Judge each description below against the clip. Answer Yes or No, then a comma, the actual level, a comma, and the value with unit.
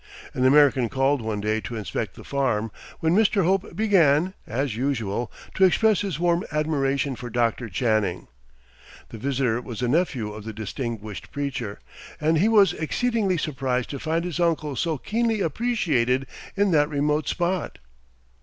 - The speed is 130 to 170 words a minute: Yes, average, 155 wpm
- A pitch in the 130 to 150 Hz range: Yes, medium, 140 Hz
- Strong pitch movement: Yes, wide, 6.3 semitones